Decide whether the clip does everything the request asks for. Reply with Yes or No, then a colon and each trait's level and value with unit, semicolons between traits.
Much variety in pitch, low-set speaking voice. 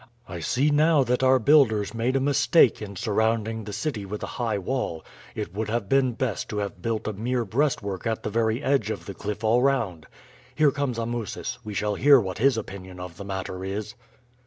No: average, 4.4 semitones; low, 110 Hz